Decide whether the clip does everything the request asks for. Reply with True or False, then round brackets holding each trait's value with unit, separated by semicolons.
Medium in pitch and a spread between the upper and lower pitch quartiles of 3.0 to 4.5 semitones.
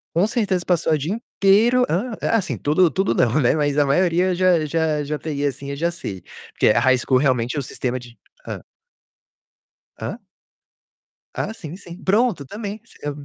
False (160 Hz; 5.3 semitones)